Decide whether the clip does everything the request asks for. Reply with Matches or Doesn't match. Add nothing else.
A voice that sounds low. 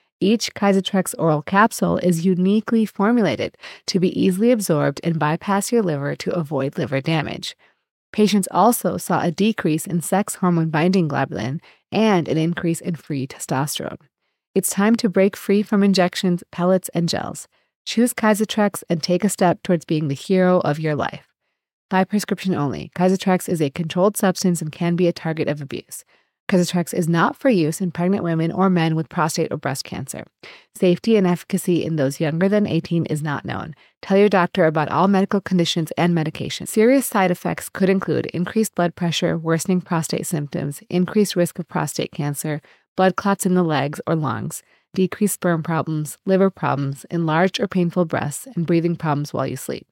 Doesn't match